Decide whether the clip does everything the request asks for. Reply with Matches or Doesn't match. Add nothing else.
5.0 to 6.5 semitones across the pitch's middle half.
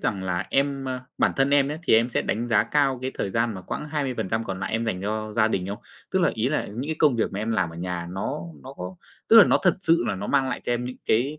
Matches